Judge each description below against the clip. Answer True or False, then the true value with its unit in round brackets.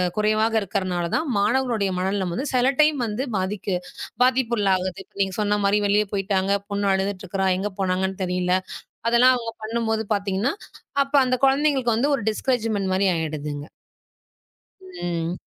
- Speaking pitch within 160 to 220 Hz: True (205 Hz)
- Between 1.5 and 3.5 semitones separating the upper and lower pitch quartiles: False (4.0 semitones)